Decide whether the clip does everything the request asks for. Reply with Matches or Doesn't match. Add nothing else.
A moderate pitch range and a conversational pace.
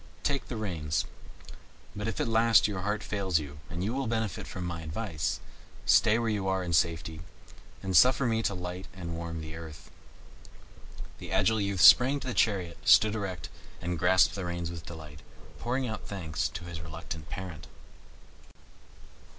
Matches